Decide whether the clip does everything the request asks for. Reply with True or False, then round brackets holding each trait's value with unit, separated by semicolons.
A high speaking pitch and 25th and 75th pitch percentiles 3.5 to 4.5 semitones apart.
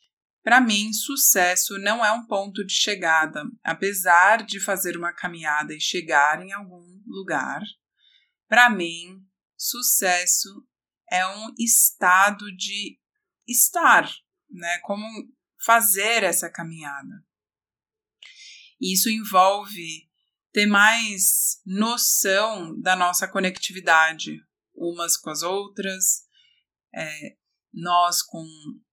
True (195 Hz; 4.1 semitones)